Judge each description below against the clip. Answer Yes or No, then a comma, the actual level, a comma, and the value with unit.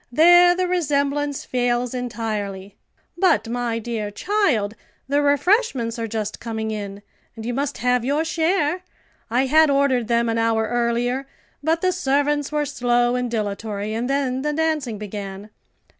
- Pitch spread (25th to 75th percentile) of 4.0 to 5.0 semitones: Yes, average, 4.6 semitones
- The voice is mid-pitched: No, high, 245 Hz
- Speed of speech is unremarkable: Yes, average, 150 wpm